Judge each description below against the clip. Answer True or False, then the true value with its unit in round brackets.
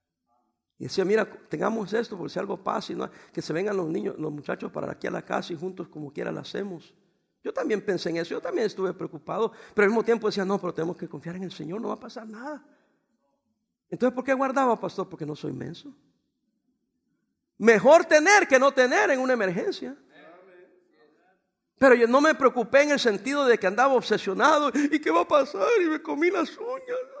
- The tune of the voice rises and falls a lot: True (6.9 semitones)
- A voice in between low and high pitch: False (225 Hz)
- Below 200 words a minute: False (205 wpm)